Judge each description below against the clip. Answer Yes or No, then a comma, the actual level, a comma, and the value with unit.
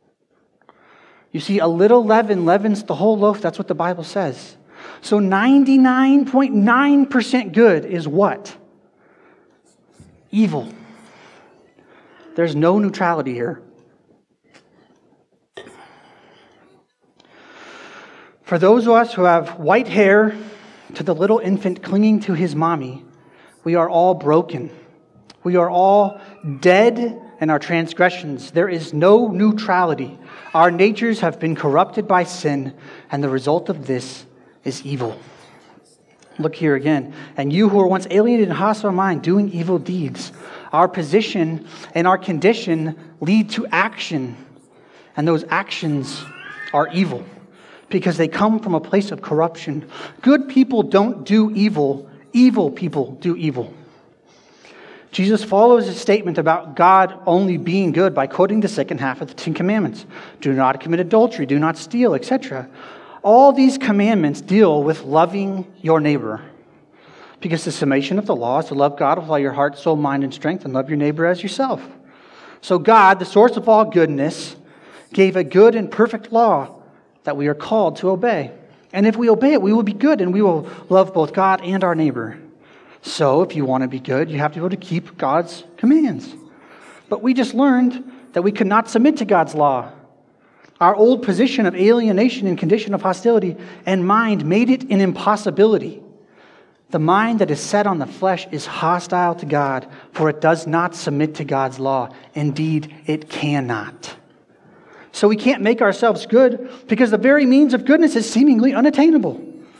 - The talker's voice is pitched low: No, medium, 185 Hz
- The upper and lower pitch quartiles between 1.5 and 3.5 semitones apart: No, average, 5.3 semitones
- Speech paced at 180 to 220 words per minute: No, average, 160 wpm